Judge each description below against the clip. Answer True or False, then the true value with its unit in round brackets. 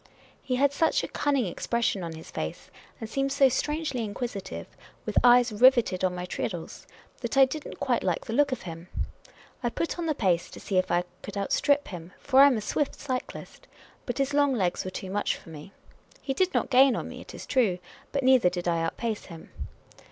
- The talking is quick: True (220 wpm)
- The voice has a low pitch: False (235 Hz)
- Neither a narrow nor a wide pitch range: False (6.8 semitones)